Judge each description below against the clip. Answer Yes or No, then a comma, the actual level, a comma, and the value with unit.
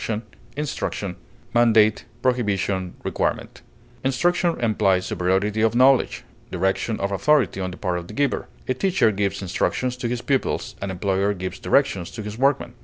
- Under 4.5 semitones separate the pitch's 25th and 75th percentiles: No, average, 5.0 semitones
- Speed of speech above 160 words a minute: No, average, 145 wpm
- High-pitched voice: No, low, 105 Hz